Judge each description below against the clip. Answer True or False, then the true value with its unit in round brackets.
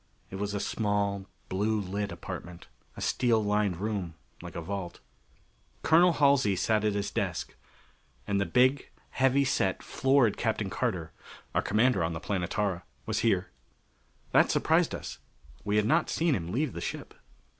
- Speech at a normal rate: True (155 wpm)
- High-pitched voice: False (105 Hz)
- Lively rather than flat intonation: False (4.3 semitones)